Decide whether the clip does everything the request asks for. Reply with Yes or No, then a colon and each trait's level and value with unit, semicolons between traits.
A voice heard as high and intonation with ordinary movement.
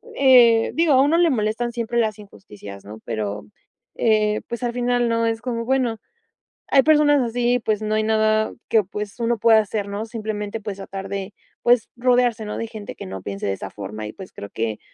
Yes: high, 220 Hz; average, 3.2 semitones